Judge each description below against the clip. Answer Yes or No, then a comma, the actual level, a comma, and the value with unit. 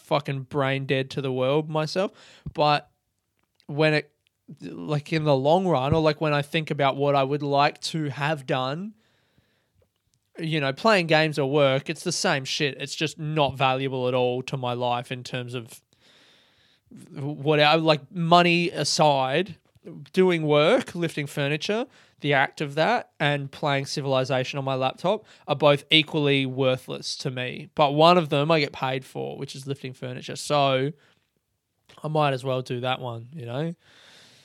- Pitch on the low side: No, medium, 145 Hz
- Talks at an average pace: Yes, average, 170 wpm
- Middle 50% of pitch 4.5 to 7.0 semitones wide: No, average, 2.8 semitones